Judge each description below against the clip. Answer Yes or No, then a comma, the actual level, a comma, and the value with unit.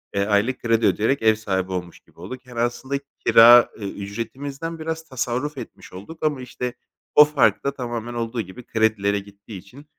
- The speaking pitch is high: No, low, 120 Hz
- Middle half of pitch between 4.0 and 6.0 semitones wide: Yes, average, 4.5 semitones